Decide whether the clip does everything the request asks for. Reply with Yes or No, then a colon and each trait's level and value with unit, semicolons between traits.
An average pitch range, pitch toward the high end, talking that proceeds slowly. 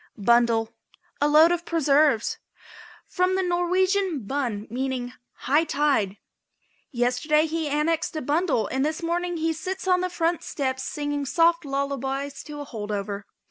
No: average, 4.5 semitones; very high, 295 Hz; average, 145 wpm